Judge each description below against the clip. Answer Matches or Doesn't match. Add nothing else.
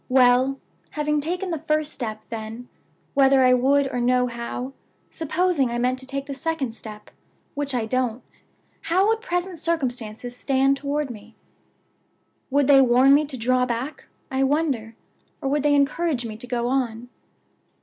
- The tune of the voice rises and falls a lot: Doesn't match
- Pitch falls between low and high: Doesn't match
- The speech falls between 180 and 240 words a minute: Doesn't match